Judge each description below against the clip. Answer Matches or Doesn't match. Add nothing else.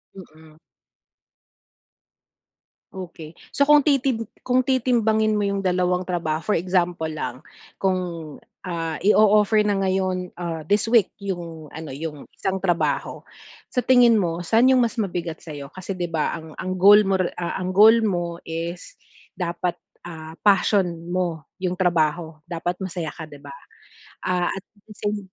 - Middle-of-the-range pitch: Matches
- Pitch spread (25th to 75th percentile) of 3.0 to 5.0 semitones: Matches